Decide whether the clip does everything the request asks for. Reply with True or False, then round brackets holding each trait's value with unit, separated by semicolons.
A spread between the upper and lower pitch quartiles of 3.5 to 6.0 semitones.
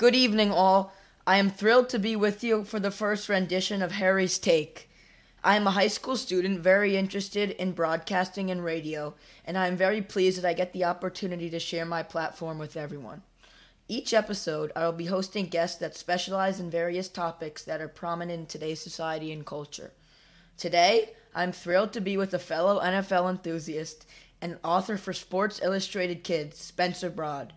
False (2.8 semitones)